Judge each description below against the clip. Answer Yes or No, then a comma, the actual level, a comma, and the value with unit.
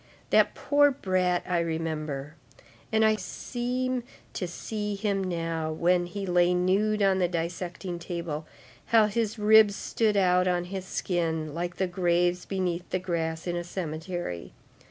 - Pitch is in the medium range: Yes, medium, 180 Hz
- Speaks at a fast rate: No, average, 150 wpm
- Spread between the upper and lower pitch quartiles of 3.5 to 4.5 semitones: No, average, 2.9 semitones